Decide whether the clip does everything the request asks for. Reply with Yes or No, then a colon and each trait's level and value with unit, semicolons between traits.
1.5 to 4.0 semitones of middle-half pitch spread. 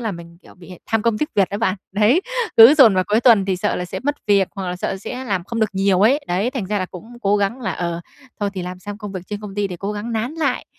Yes: average, 3.4 semitones